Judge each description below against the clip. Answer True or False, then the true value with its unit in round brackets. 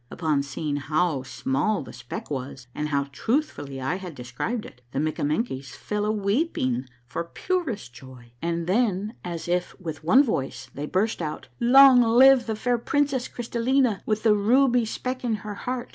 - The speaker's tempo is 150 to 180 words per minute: True (175 wpm)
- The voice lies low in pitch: False (195 Hz)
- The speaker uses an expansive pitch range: True (8.9 semitones)